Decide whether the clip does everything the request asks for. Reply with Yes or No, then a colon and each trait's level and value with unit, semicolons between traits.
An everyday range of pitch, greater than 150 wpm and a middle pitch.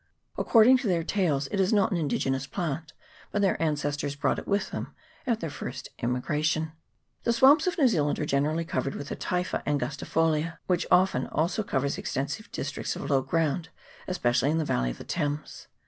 Yes: average, 4.7 semitones; average, 190 wpm; medium, 160 Hz